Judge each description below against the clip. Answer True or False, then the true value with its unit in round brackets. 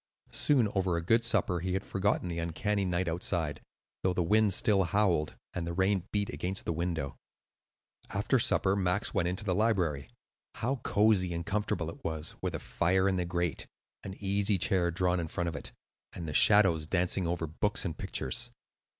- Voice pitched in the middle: False (90 Hz)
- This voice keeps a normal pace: True (185 wpm)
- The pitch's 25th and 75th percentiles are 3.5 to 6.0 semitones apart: False (3.0 semitones)